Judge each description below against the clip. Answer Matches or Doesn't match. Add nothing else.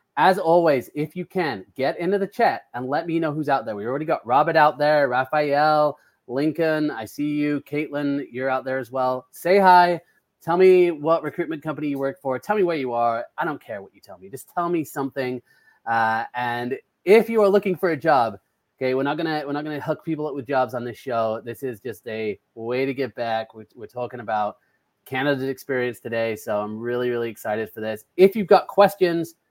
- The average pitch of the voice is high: Doesn't match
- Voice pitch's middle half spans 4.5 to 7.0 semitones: Matches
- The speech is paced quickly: Matches